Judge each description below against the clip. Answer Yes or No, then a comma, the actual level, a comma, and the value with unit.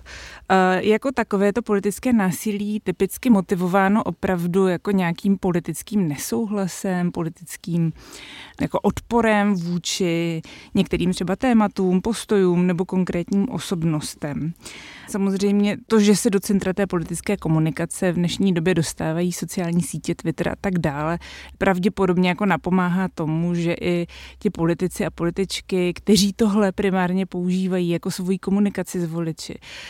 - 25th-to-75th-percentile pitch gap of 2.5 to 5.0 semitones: Yes, average, 2.8 semitones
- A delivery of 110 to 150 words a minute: Yes, average, 125 wpm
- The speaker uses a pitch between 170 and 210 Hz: Yes, medium, 185 Hz